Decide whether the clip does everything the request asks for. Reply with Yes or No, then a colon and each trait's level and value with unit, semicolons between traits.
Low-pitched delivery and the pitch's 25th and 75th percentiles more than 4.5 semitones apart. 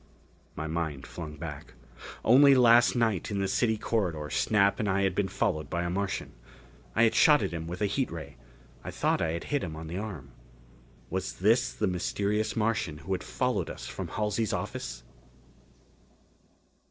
Yes: very low, 95 Hz; average, 5.1 semitones